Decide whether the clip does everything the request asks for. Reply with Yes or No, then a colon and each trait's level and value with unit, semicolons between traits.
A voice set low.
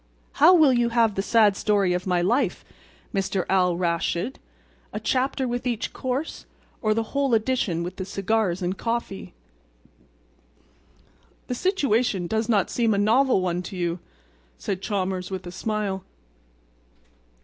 No: high, 210 Hz